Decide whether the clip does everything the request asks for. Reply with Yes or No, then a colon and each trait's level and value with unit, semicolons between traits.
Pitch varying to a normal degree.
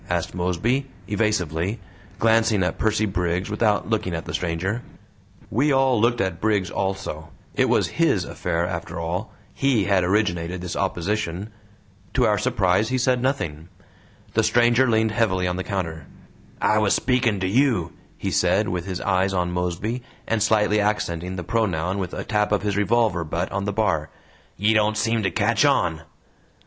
Yes: average, 3.7 semitones